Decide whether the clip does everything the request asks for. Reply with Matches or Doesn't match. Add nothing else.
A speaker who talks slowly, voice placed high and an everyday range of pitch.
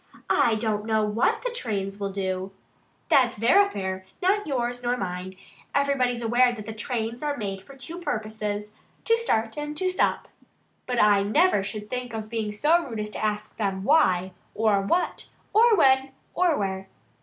Doesn't match